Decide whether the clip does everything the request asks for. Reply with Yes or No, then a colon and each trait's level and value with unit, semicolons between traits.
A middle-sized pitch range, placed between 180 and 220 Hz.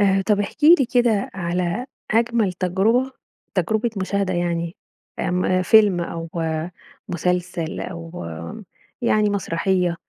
Yes: average, 3.5 semitones; medium, 185 Hz